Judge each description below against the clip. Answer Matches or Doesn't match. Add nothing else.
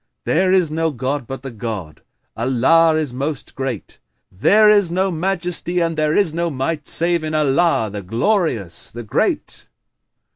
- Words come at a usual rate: Matches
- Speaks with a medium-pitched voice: Matches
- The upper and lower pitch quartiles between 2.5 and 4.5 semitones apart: Doesn't match